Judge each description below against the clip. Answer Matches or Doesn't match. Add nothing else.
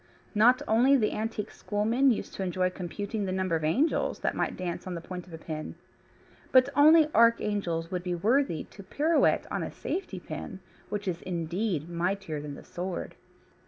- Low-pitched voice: Doesn't match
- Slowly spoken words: Doesn't match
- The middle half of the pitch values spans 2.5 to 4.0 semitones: Doesn't match